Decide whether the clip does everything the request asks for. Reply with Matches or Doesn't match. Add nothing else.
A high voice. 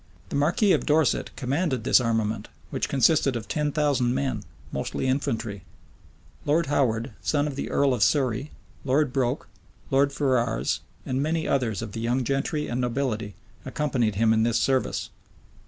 Doesn't match